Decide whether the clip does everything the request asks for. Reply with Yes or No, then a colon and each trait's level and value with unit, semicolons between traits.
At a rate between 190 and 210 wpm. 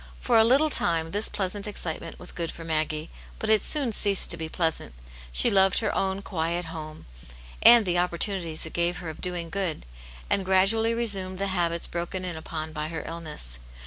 Yes: average, 195 wpm